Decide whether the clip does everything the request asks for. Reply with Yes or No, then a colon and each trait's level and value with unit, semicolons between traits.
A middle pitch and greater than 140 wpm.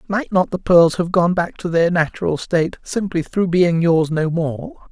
Yes: medium, 170 Hz; fast, 205 wpm